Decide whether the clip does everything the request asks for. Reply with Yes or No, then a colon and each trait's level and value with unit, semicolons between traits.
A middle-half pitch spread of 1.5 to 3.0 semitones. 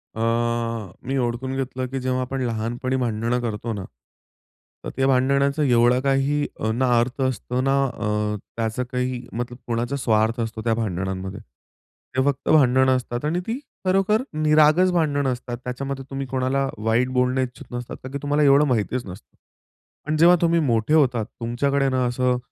Yes: average, 2.7 semitones